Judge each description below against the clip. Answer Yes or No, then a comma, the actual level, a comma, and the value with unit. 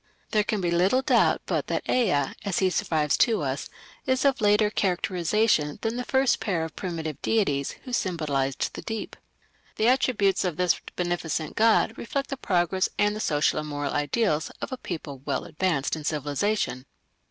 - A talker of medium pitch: Yes, medium, 180 Hz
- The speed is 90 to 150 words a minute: No, average, 175 wpm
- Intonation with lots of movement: Yes, wide, 6.2 semitones